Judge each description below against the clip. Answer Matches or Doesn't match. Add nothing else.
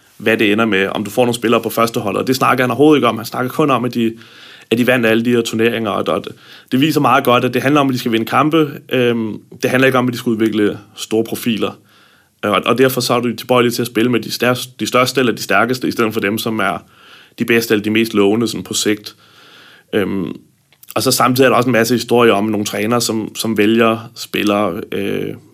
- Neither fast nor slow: Doesn't match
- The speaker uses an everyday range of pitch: Doesn't match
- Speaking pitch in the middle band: Doesn't match